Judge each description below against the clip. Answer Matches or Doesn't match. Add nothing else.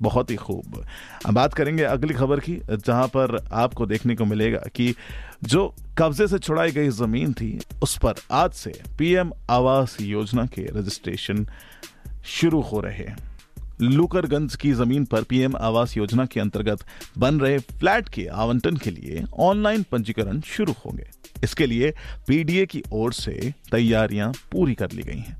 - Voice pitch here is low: Matches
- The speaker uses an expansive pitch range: Doesn't match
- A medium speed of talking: Matches